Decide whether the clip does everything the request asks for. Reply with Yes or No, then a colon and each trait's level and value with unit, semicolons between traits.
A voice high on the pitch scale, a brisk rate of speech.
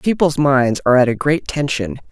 No: low, 135 Hz; fast, 225 wpm